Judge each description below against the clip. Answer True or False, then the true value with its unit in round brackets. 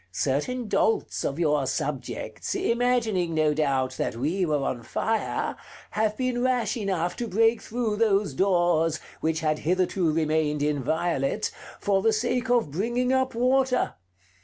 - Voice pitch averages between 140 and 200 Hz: True (185 Hz)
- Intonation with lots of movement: True (7.4 semitones)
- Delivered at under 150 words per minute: True (140 wpm)